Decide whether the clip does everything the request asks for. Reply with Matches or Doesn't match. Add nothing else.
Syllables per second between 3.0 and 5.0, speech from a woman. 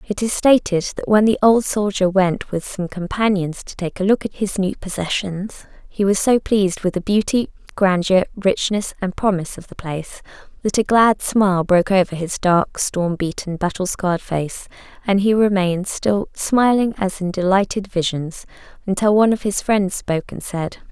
Matches